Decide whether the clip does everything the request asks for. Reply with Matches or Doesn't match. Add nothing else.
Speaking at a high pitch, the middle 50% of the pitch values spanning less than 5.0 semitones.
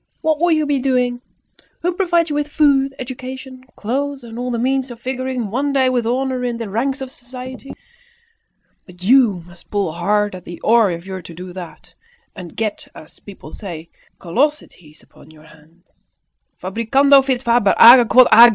Doesn't match